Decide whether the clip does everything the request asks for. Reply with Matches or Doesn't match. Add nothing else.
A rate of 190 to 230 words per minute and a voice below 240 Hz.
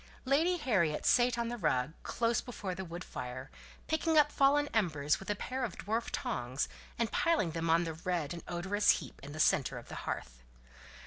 Matches